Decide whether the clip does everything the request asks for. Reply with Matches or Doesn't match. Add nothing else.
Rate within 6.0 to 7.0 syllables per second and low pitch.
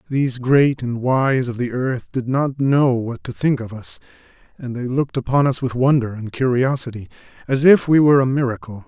Doesn't match